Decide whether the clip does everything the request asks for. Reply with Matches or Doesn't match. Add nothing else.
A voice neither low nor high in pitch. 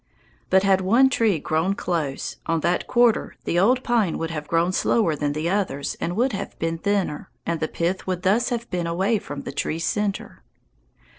Matches